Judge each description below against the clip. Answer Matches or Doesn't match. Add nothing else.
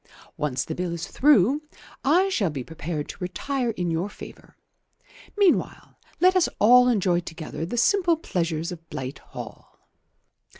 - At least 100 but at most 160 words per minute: Matches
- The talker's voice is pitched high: Doesn't match